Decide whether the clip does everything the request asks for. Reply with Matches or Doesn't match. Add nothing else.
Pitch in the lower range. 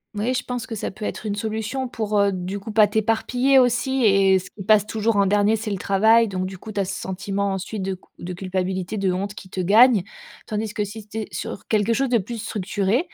Doesn't match